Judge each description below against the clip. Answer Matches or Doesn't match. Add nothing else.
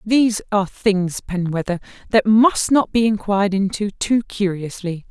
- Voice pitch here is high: Matches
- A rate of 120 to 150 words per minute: Matches